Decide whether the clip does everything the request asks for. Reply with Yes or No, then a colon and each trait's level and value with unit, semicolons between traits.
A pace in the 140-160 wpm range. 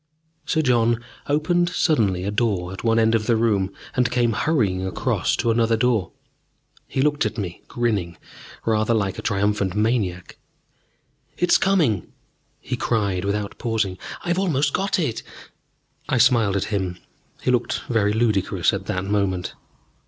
Yes: average, 150 wpm